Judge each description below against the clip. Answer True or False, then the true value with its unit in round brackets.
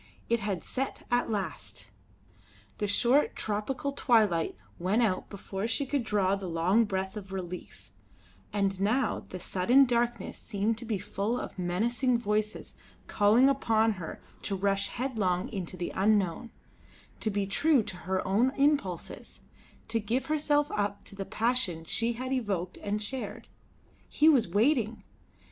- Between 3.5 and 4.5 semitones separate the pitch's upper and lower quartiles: True (4.0 semitones)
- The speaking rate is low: False (150 wpm)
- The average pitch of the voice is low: False (210 Hz)